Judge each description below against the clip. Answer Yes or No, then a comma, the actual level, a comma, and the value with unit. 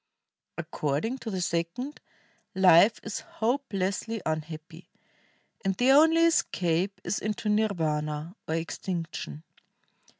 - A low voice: No, medium, 185 Hz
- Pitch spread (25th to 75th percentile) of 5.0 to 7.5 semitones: Yes, wide, 5.5 semitones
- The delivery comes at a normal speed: No, slow, 100 wpm